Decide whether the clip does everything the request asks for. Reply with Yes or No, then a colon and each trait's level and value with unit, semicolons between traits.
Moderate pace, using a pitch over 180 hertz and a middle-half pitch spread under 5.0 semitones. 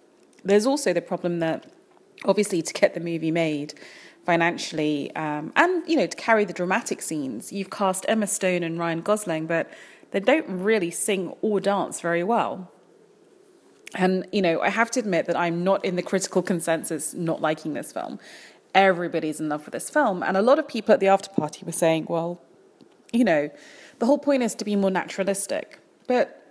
No: average, 190 wpm; high, 190 Hz; wide, 5.5 semitones